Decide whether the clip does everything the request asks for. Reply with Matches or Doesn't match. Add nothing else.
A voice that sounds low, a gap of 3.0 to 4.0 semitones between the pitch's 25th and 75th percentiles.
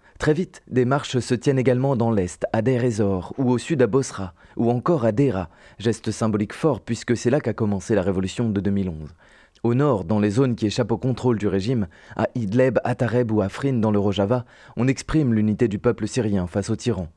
Matches